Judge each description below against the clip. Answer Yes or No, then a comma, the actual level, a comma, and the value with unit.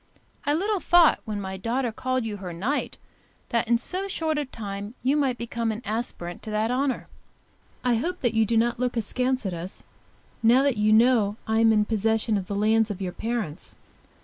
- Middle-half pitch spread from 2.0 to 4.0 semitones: Yes, average, 3.3 semitones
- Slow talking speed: No, average, 200 wpm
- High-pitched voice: Yes, high, 225 Hz